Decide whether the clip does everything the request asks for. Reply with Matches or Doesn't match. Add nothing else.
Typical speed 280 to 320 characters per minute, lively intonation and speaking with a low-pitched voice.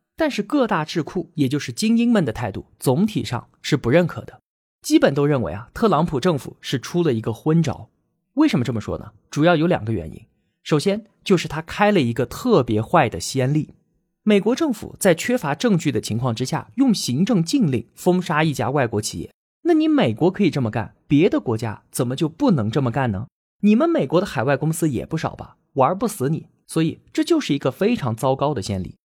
Doesn't match